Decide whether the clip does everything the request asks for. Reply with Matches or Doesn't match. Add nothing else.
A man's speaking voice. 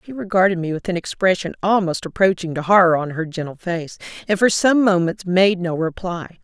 Doesn't match